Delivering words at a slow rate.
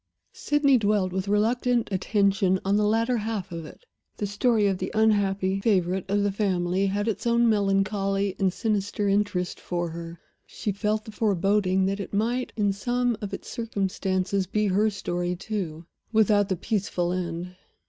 No: average, 165 wpm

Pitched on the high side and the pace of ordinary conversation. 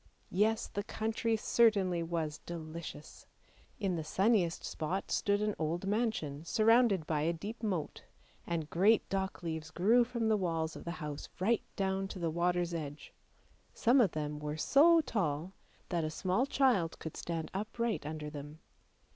No: medium, 180 Hz; average, 160 wpm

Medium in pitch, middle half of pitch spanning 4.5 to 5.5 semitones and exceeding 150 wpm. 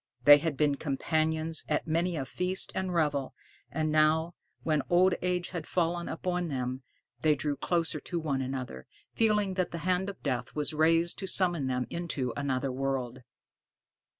No: medium, 155 Hz; average, 4.1 semitones; average, 165 wpm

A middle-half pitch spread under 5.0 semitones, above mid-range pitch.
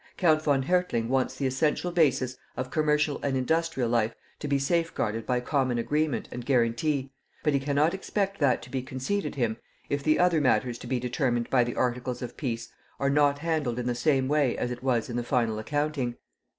No: average, 3.5 semitones; low, 135 Hz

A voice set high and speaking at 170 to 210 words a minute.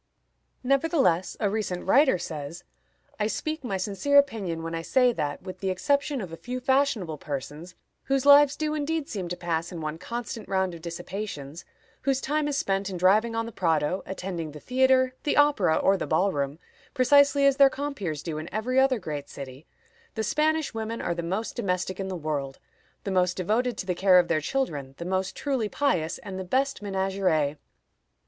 Yes: high, 195 Hz; average, 190 wpm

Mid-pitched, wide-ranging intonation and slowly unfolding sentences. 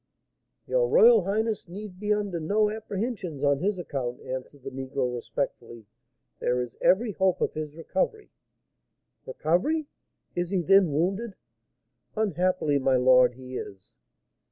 Yes: medium, 175 Hz; wide, 7.7 semitones; slow, 130 wpm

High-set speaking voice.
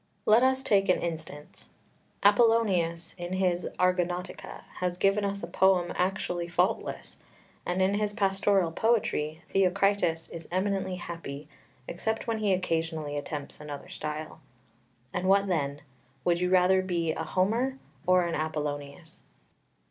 No: medium, 180 Hz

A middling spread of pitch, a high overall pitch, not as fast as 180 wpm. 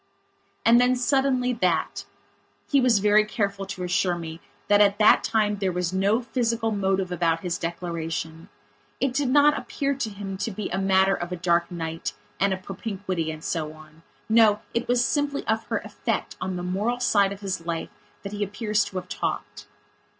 No: average, 4.1 semitones; high, 195 Hz; average, 185 wpm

